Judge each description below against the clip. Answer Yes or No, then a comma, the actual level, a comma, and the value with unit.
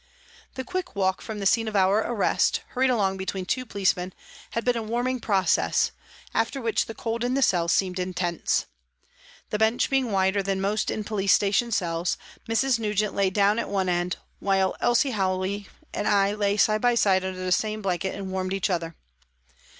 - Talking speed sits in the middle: Yes, average, 190 wpm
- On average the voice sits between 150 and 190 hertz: No, high, 200 Hz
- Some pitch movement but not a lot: Yes, average, 3.1 semitones